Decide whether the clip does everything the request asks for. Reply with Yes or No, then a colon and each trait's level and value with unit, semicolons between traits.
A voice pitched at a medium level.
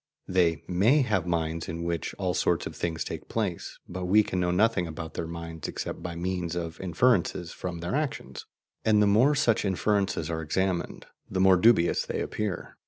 No: very low, 90 Hz